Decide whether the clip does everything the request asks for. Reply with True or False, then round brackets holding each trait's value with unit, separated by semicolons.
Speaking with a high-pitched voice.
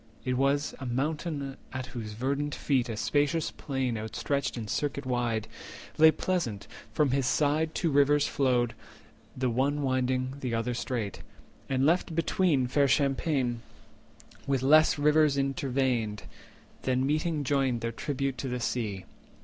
False (135 Hz)